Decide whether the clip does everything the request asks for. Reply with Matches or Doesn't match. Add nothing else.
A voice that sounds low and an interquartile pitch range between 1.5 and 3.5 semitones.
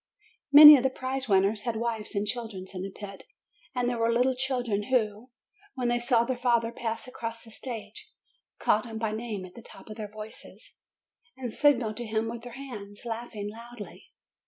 Doesn't match